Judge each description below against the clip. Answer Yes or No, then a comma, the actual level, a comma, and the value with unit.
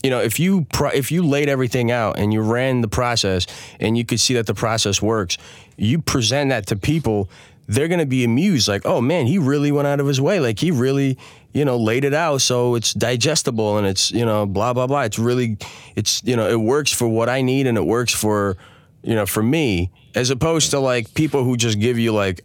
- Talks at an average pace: No, fast, 240 wpm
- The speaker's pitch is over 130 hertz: No, low, 120 Hz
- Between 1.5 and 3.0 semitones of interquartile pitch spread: No, average, 4.1 semitones